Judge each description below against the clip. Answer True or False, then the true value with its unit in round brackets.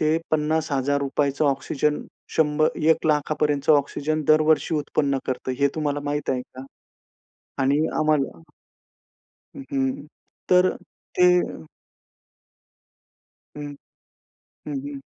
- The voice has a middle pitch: True (145 Hz)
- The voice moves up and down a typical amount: False (1.7 semitones)